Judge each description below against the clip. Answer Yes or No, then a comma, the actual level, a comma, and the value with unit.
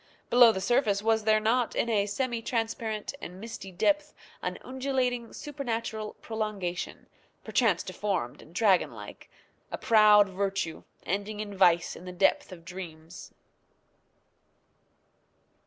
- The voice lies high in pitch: Yes, high, 210 Hz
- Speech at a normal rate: No, slow, 125 wpm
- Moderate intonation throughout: Yes, average, 3.7 semitones